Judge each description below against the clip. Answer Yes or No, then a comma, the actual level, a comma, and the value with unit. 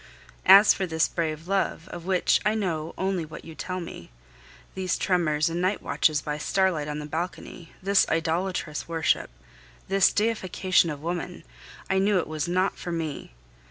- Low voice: No, medium, 175 Hz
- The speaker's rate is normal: Yes, average, 165 wpm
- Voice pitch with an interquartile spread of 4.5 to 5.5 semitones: No, average, 3.1 semitones